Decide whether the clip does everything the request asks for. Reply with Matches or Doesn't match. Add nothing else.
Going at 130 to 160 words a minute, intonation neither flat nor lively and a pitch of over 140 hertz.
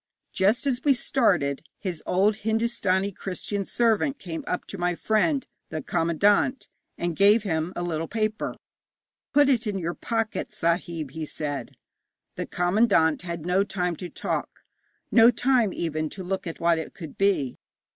Matches